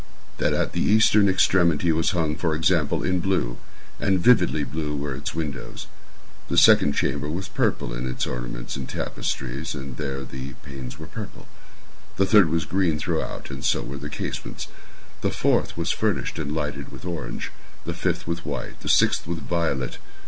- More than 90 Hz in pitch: No, very low, 80 Hz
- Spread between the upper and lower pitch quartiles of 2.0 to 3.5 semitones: No, average, 4.2 semitones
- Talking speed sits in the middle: Yes, average, 165 wpm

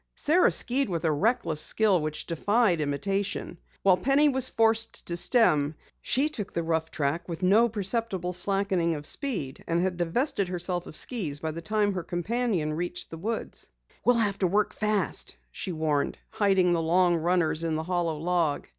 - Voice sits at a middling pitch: Yes, medium, 180 Hz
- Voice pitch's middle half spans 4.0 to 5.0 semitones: Yes, average, 4.6 semitones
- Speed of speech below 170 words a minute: No, average, 175 wpm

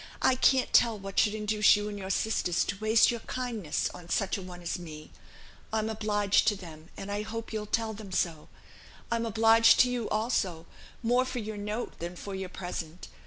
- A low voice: No, high, 210 Hz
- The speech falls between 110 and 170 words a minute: No, average, 200 wpm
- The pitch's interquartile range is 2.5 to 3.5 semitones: Yes, average, 3.2 semitones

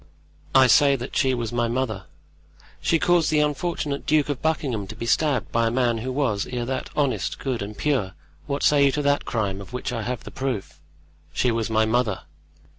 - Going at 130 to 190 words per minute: No, fast, 205 wpm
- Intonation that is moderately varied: Yes, average, 3.9 semitones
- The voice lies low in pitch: Yes, low, 125 Hz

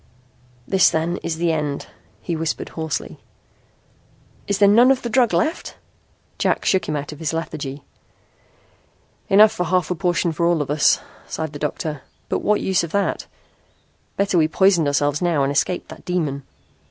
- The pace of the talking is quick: No, average, 170 wpm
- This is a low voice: No, medium, 165 Hz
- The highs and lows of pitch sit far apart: No, average, 4.0 semitones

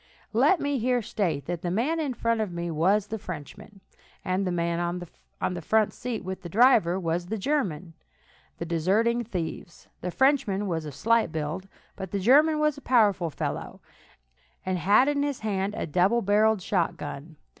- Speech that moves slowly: No, average, 175 wpm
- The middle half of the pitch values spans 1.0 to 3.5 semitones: No, average, 5.2 semitones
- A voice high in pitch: Yes, high, 195 Hz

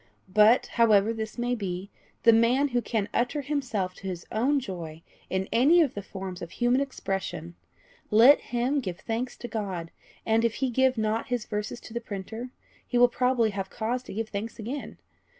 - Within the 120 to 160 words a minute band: No, average, 185 wpm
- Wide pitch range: No, average, 3.8 semitones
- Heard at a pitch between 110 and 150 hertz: No, high, 225 Hz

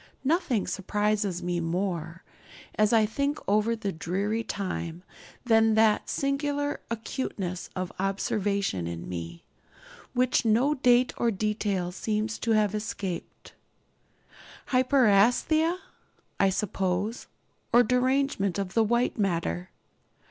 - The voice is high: Yes, high, 210 Hz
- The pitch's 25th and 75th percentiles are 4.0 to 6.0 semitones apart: Yes, average, 4.5 semitones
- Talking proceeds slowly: Yes, slow, 110 wpm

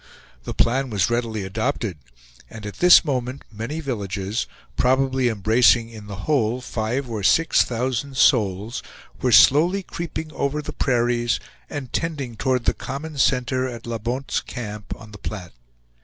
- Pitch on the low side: Yes, low, 120 Hz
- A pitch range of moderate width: Yes, average, 3.7 semitones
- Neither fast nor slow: Yes, average, 150 wpm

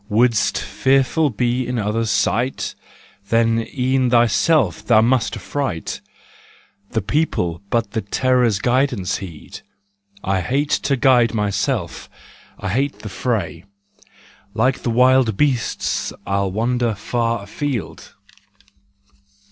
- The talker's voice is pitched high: No, low, 115 Hz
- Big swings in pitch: No, average, 3.8 semitones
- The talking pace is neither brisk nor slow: No, slow, 110 wpm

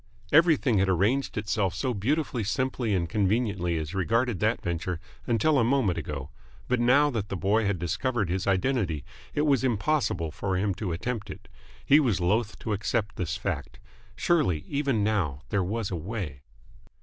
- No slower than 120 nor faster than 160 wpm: No, average, 170 wpm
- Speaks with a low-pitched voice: Yes, low, 105 Hz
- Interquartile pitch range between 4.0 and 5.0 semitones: No, wide, 5.5 semitones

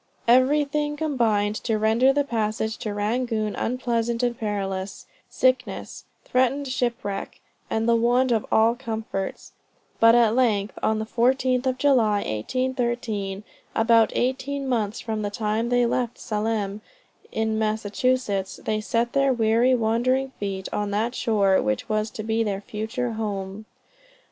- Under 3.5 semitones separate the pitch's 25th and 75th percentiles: Yes, average, 3.0 semitones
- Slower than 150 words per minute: Yes, average, 140 wpm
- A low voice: No, high, 225 Hz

